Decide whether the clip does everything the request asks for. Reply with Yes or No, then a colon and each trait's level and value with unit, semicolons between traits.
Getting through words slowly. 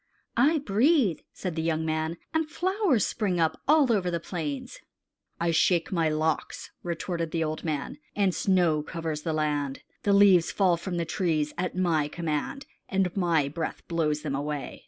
No: average, 170 wpm